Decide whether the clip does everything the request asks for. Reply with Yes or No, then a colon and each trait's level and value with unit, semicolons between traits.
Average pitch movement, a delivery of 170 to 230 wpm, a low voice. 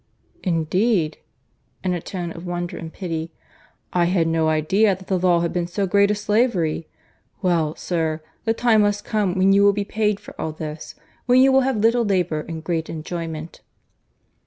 No: average, 3.9 semitones; average, 180 wpm; medium, 180 Hz